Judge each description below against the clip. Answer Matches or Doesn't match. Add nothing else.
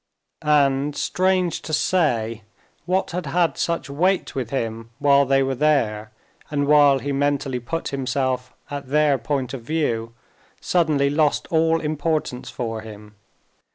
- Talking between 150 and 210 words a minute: Doesn't match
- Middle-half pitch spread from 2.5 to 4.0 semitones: Matches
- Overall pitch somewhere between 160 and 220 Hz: Doesn't match